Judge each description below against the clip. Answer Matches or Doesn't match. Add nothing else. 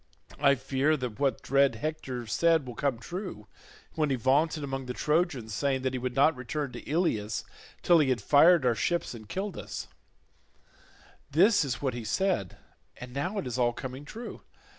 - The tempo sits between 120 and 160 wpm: Doesn't match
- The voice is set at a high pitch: Doesn't match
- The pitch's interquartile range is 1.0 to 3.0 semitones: Doesn't match